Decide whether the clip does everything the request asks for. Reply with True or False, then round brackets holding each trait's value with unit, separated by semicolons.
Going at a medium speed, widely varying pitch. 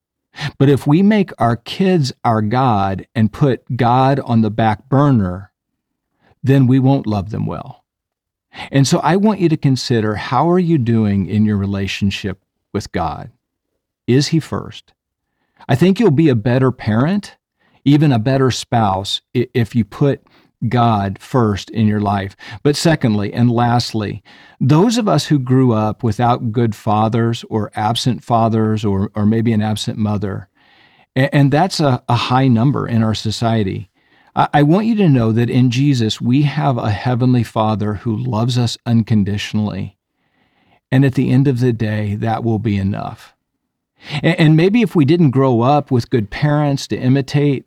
False (165 wpm; 4.4 semitones)